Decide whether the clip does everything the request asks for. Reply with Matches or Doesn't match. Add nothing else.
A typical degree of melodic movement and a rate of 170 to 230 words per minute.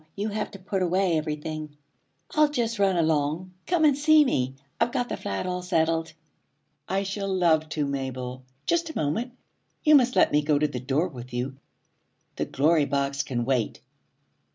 Doesn't match